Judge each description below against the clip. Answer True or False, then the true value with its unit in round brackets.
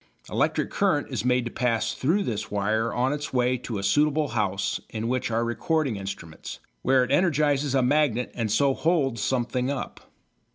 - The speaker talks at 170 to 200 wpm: True (175 wpm)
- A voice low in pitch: True (125 Hz)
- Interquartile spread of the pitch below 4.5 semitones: True (4.1 semitones)